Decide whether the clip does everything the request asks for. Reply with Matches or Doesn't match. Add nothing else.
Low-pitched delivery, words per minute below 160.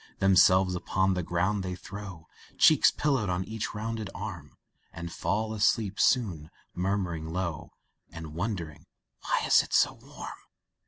Matches